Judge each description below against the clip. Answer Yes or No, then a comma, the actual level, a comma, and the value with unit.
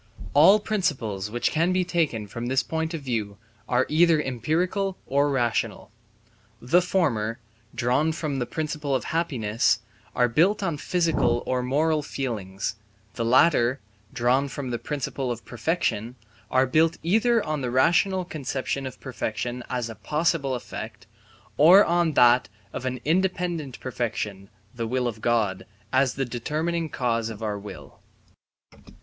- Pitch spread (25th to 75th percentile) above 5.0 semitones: Yes, wide, 5.4 semitones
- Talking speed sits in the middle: Yes, average, 145 wpm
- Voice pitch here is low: Yes, low, 130 Hz